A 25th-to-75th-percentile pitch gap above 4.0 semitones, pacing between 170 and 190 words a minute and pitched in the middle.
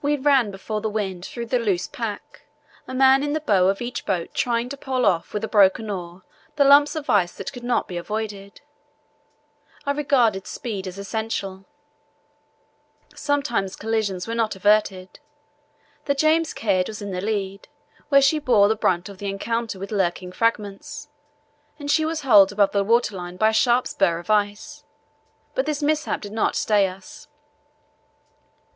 No: average, 4.9 semitones; average, 175 wpm; high, 215 Hz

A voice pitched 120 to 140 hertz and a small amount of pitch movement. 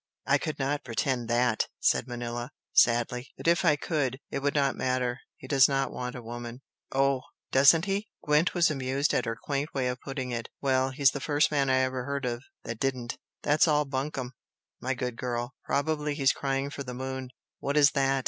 Yes: low, 135 Hz; narrow, 2.3 semitones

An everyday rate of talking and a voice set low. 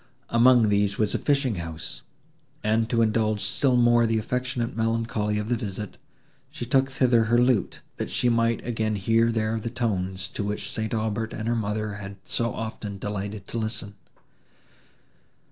Yes: average, 165 wpm; low, 110 Hz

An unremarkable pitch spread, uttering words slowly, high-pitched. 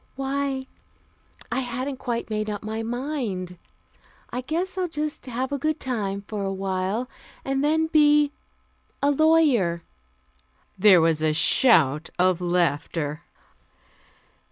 No: wide, 7.3 semitones; slow, 125 wpm; high, 235 Hz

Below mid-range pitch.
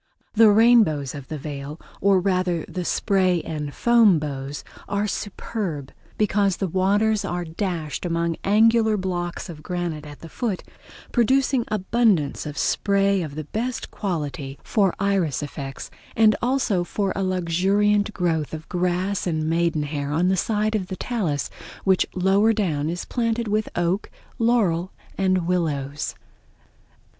No: medium, 185 Hz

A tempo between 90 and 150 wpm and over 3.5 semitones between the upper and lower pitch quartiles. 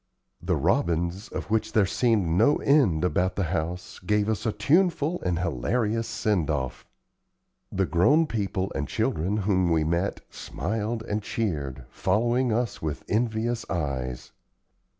Yes: average, 140 wpm; average, 5.0 semitones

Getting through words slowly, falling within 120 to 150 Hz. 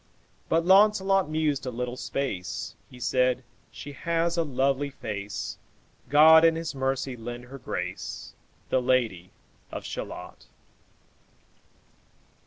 Yes: slow, 115 wpm; low, 135 Hz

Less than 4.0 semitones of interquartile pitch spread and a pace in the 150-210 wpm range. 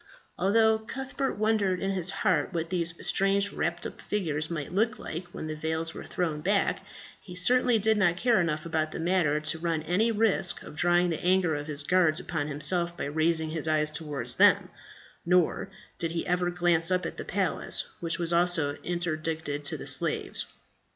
Yes: average, 3.1 semitones; average, 185 wpm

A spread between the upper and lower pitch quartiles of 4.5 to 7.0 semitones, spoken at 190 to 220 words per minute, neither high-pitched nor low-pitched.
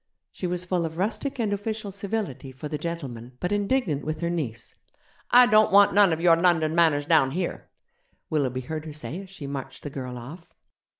Yes: wide, 5.4 semitones; average, 195 wpm; medium, 165 Hz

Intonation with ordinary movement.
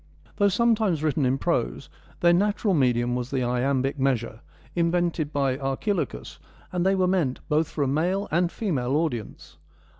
No: wide, 5.7 semitones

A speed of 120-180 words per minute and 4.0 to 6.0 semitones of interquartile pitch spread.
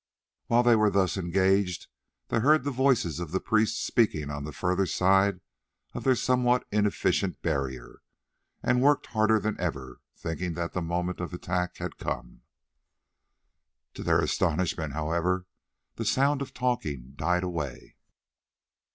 Yes: average, 140 wpm; average, 5.1 semitones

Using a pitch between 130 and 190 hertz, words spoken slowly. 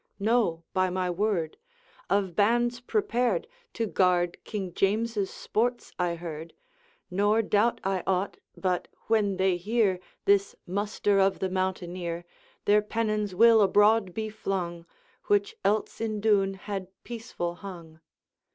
No: high, 200 Hz; slow, 130 wpm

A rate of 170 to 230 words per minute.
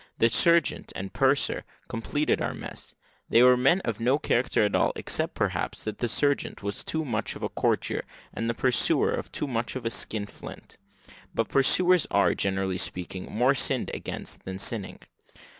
Yes: average, 175 wpm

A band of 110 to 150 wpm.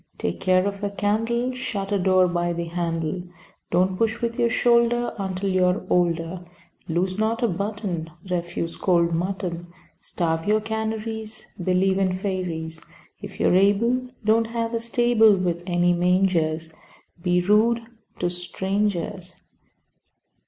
Yes: average, 140 wpm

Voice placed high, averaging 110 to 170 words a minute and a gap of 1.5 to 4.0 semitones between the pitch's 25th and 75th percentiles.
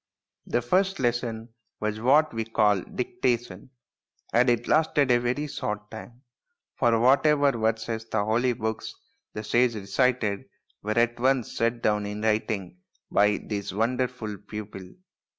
No: low, 115 Hz; average, 145 wpm; average, 2.8 semitones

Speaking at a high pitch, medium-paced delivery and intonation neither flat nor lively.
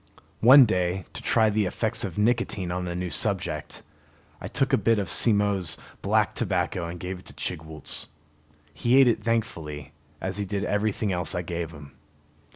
No: very low, 95 Hz; average, 175 wpm; average, 3.9 semitones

